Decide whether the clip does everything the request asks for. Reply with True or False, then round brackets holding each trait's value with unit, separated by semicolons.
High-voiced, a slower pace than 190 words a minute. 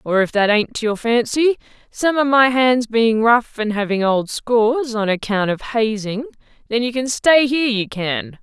False (230 Hz; 200 wpm)